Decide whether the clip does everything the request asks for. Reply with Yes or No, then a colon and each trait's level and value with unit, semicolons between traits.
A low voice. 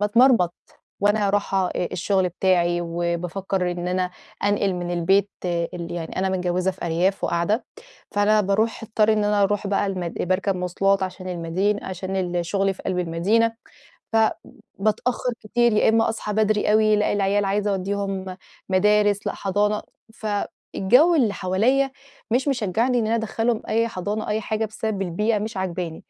No: high, 200 Hz